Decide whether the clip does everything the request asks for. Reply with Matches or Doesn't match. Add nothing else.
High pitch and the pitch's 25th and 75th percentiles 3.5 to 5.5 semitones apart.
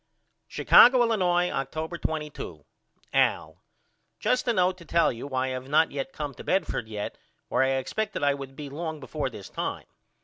Doesn't match